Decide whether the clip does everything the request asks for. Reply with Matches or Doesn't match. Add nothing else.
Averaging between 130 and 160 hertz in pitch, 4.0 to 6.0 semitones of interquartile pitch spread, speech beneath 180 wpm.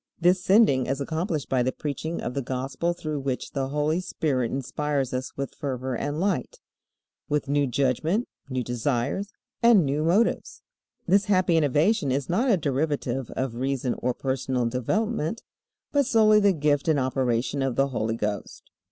Matches